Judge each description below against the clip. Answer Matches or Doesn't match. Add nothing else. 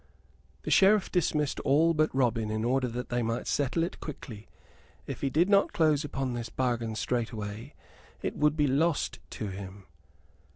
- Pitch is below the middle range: Matches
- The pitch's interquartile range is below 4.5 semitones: Doesn't match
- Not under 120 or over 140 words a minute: Doesn't match